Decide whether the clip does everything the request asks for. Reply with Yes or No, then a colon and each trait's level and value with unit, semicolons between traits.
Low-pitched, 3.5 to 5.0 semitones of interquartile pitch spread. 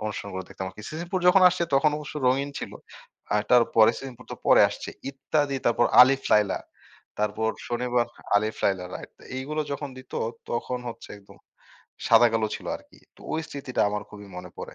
Yes: low, 120 Hz; average, 4.6 semitones